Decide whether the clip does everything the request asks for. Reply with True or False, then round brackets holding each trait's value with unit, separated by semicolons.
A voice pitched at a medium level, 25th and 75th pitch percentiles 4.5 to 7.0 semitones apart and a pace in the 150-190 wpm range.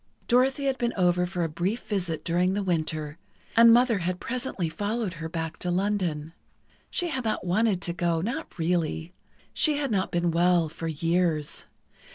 True (180 Hz; 5.1 semitones; 170 wpm)